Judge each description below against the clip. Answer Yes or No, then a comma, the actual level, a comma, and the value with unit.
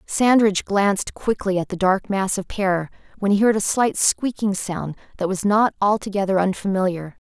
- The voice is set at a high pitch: Yes, high, 195 Hz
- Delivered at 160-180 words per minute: Yes, average, 175 wpm